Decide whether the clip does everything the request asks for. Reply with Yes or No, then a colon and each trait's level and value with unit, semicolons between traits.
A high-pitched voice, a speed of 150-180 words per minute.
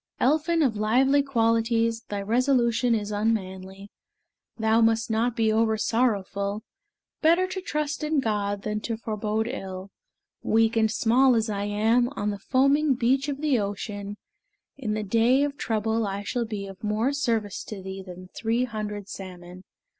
Yes: high, 225 Hz; average, 155 wpm